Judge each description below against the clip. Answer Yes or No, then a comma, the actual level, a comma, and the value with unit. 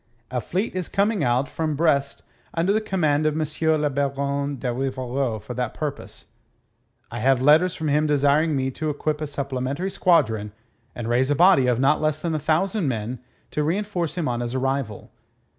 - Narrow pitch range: No, average, 3.5 semitones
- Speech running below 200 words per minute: Yes, average, 185 wpm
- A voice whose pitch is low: No, medium, 145 Hz